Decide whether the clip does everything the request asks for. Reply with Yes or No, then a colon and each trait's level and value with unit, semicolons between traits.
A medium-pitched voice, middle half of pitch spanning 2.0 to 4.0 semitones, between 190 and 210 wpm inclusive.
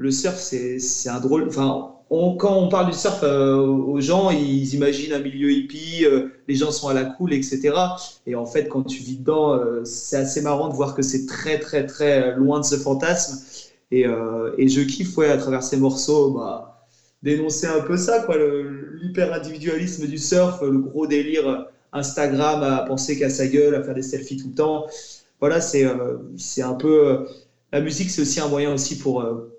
Yes: medium, 145 Hz; narrow, 2.4 semitones; average, 205 wpm